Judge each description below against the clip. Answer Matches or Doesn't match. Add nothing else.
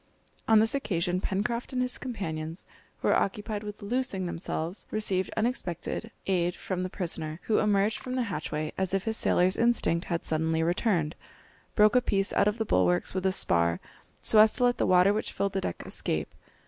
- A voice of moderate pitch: Doesn't match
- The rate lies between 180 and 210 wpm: Matches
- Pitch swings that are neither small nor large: Matches